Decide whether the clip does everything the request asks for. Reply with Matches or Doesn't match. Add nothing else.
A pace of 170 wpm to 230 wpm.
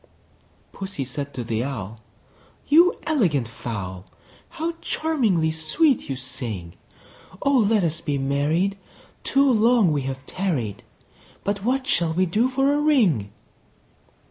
Doesn't match